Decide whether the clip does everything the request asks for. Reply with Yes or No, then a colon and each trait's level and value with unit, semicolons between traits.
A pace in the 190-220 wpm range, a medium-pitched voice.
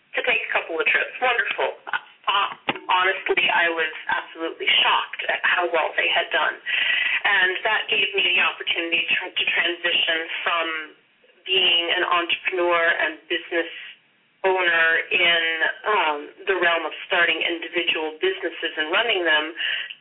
No: average, 140 wpm; medium, 170 Hz